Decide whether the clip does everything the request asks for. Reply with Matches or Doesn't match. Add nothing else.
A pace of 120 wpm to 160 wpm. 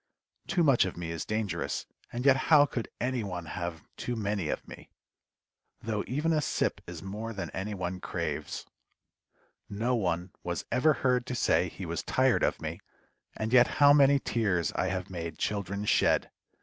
Doesn't match